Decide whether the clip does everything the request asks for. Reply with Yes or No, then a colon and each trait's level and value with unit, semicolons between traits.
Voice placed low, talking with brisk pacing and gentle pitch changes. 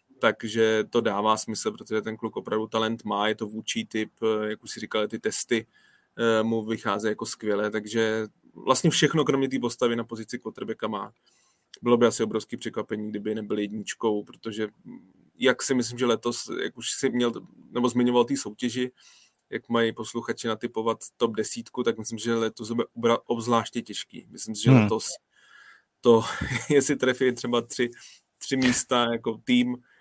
No: low, 115 Hz; average, 160 wpm; narrow, 1.9 semitones